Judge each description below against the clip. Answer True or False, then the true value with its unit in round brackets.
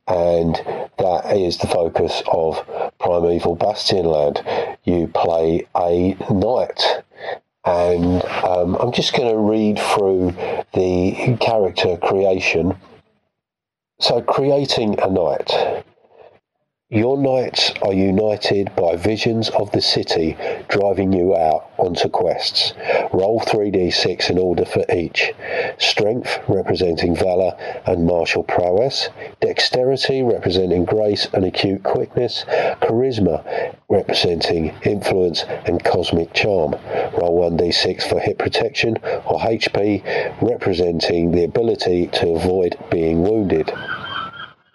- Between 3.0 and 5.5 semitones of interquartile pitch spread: True (3.4 semitones)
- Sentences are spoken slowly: True (105 wpm)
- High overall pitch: False (90 Hz)